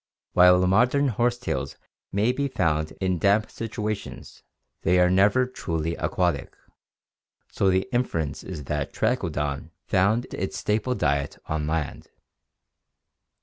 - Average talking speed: No, slow, 115 wpm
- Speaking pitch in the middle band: No, very low, 95 Hz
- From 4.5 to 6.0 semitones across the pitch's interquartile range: Yes, wide, 5.6 semitones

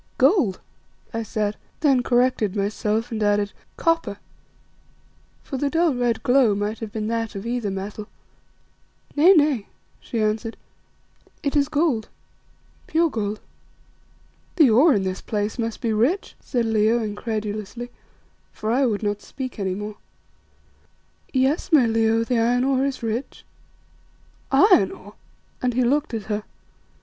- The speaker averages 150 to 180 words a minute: No, average, 140 wpm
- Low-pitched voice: No, high, 230 Hz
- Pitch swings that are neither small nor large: Yes, average, 3.8 semitones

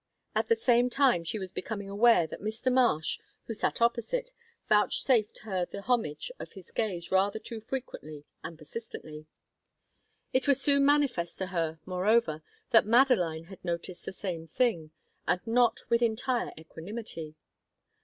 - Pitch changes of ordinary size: No, wide, 5.8 semitones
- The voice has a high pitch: Yes, high, 215 Hz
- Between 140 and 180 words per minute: Yes, average, 150 wpm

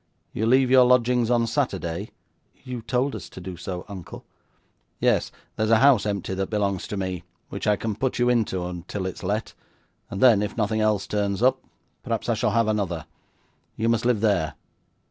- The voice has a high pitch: No, low, 105 Hz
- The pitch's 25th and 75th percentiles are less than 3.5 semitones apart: No, average, 3.9 semitones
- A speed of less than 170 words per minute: No, average, 195 wpm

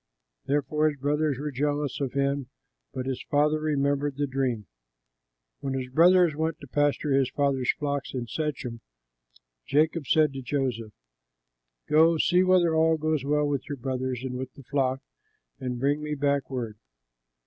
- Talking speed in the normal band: Yes, average, 160 wpm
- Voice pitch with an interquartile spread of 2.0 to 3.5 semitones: Yes, narrow, 2.4 semitones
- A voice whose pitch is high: No, medium, 140 Hz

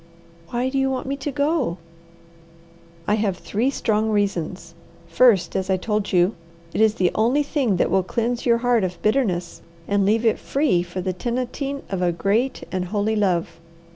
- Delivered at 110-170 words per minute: No, average, 180 wpm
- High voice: Yes, high, 215 Hz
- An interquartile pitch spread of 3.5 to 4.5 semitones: No, average, 4.9 semitones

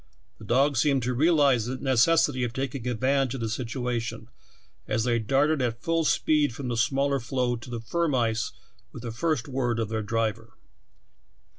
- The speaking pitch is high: No, low, 125 Hz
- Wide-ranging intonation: No, average, 3.1 semitones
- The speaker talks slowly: No, average, 175 wpm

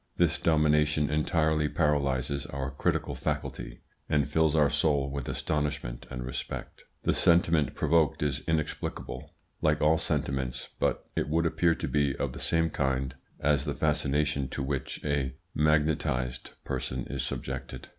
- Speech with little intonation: Yes, narrow, 2.3 semitones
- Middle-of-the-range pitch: No, very low, 75 Hz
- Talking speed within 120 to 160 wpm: Yes, average, 145 wpm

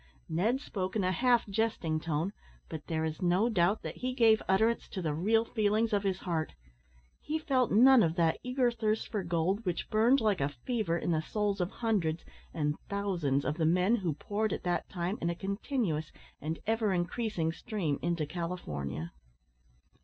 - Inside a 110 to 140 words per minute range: No, average, 185 wpm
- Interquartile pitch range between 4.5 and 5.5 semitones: Yes, average, 5.1 semitones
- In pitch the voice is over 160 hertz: Yes, high, 190 Hz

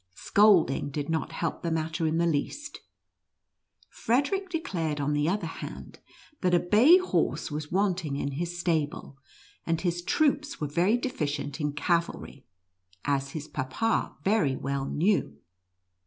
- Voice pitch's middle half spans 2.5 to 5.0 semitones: No, wide, 5.4 semitones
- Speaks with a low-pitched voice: No, medium, 165 Hz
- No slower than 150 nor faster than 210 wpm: No, average, 140 wpm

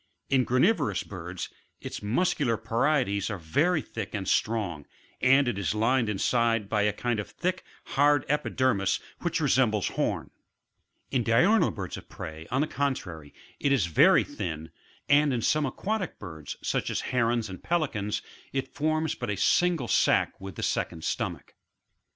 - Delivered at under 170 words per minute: Yes, average, 155 wpm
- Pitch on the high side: No, low, 115 Hz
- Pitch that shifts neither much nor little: No, wide, 6.3 semitones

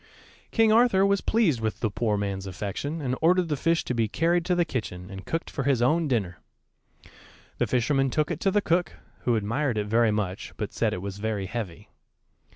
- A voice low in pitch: Yes, low, 125 Hz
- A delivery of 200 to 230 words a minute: Yes, fast, 205 wpm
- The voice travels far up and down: Yes, wide, 8.0 semitones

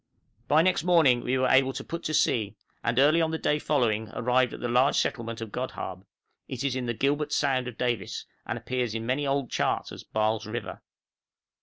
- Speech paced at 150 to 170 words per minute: No, fast, 205 wpm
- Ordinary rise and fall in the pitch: Yes, average, 3.5 semitones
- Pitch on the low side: Yes, low, 125 Hz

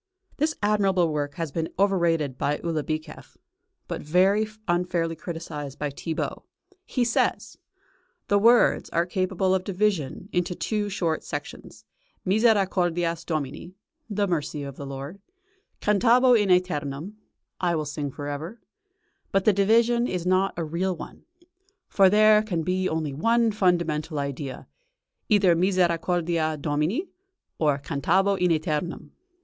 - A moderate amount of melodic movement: Yes, average, 4.3 semitones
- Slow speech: Yes, slow, 130 wpm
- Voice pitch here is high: No, medium, 175 Hz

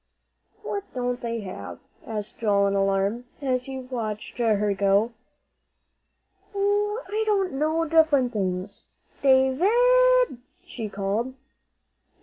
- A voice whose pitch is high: Yes, very high, 250 Hz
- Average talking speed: No, slow, 115 wpm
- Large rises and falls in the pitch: Yes, wide, 7.9 semitones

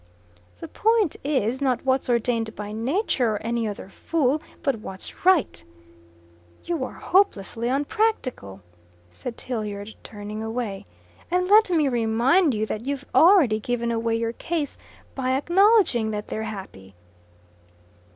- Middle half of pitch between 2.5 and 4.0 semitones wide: No, wide, 5.4 semitones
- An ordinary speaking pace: No, slow, 130 wpm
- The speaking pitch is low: No, high, 240 Hz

